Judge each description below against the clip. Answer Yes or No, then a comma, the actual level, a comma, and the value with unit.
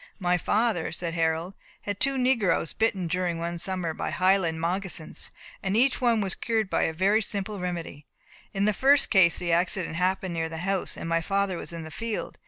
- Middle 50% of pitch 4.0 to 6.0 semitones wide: No, average, 3.4 semitones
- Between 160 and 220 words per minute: Yes, average, 190 wpm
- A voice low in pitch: No, medium, 185 Hz